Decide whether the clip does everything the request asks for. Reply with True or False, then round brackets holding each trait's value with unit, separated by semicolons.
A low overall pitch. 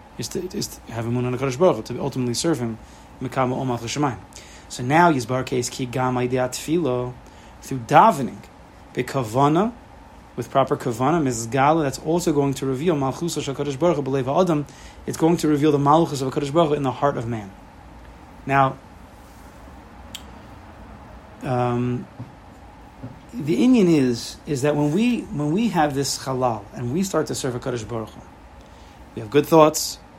True (130 Hz)